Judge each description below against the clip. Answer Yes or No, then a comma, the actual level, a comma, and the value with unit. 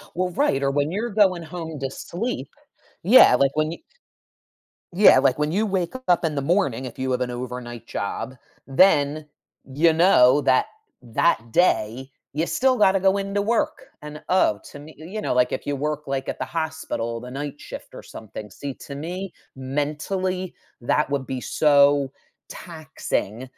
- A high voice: No, medium, 150 Hz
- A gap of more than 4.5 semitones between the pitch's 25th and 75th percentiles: Yes, average, 5.3 semitones